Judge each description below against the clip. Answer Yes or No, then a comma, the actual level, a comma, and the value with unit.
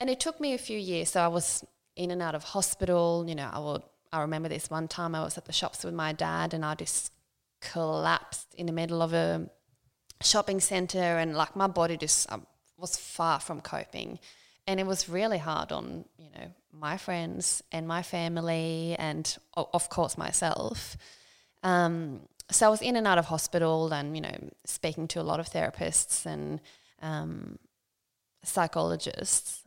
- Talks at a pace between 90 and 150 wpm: No, average, 185 wpm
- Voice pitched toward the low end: No, medium, 165 Hz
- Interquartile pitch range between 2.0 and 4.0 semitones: Yes, average, 2.7 semitones